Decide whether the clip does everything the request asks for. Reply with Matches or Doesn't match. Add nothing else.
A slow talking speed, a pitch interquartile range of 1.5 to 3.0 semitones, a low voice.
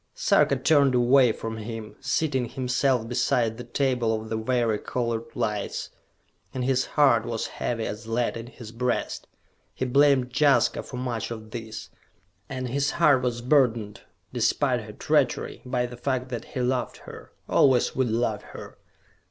Doesn't match